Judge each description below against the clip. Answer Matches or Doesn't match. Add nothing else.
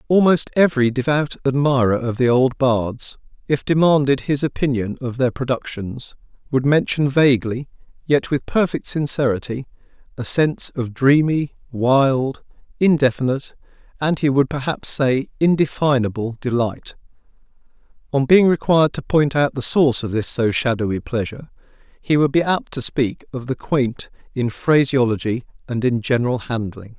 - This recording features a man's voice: Matches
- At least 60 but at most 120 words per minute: Doesn't match